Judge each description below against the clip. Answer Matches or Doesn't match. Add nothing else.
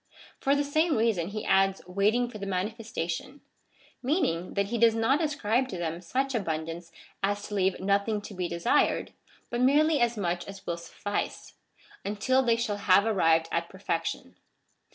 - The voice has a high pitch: Matches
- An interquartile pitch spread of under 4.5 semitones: Doesn't match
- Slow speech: Doesn't match